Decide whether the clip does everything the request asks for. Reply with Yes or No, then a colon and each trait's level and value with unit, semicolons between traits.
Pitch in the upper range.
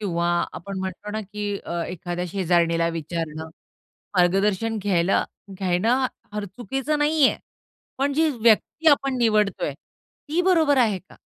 Yes: high, 205 Hz